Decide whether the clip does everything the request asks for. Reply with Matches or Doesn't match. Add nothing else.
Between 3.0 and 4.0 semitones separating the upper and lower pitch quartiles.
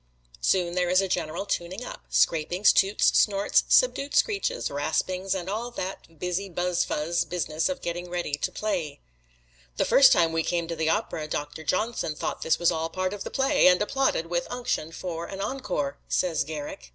Matches